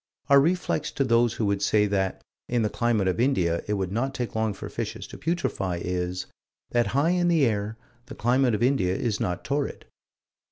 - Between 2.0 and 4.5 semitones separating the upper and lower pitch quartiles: No, wide, 5.6 semitones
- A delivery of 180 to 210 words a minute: Yes, average, 200 wpm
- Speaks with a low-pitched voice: Yes, low, 115 Hz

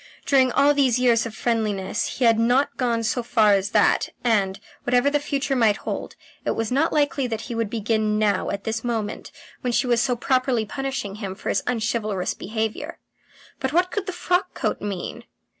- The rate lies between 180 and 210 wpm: Yes, average, 190 wpm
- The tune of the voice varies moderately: Yes, average, 3.6 semitones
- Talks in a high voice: Yes, high, 235 Hz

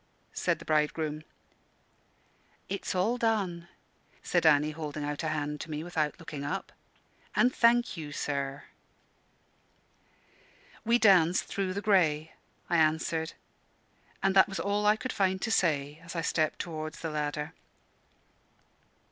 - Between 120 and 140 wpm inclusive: Yes, slow, 135 wpm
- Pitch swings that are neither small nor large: Yes, average, 4.2 semitones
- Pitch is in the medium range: Yes, medium, 165 Hz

